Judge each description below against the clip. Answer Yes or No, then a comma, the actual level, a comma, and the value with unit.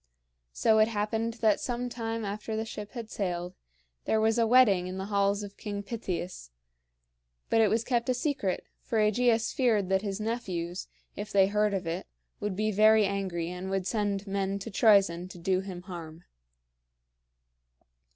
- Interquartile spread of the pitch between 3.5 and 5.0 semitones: No, average, 2.8 semitones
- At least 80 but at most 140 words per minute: No, average, 170 wpm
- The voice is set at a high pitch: Yes, high, 205 Hz